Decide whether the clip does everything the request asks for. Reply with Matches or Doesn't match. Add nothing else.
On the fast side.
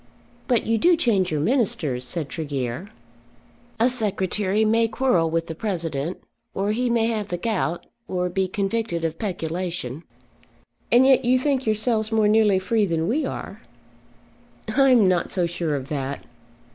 Doesn't match